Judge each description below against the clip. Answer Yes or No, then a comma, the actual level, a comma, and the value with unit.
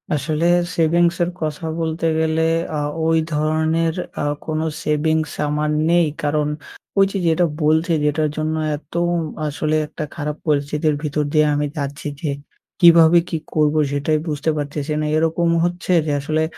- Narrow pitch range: Yes, narrow, 1.5 semitones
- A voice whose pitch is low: No, medium, 155 Hz